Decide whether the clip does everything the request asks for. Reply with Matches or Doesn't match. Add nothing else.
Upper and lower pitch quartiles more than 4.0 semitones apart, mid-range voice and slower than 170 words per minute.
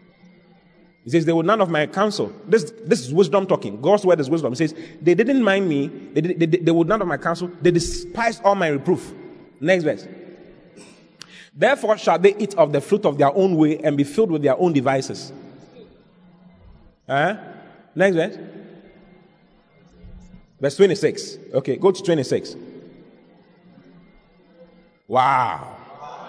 Doesn't match